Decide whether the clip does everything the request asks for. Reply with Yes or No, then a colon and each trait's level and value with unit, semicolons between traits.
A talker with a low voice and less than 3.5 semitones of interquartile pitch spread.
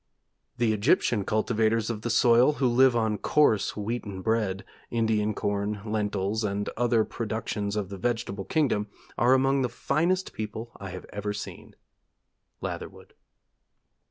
Yes: low, 110 Hz; narrow, 2.6 semitones